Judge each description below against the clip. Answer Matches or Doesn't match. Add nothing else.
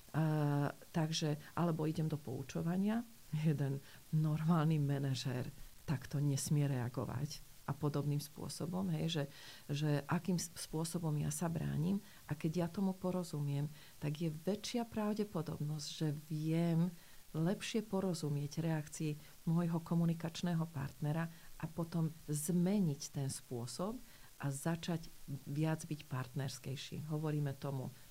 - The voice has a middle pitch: Matches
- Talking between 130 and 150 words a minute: Doesn't match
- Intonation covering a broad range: Doesn't match